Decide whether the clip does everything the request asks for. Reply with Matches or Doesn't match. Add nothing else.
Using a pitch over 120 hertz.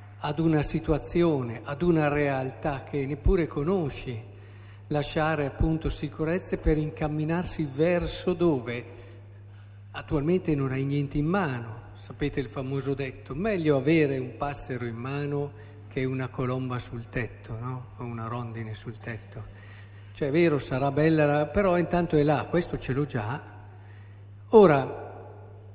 Matches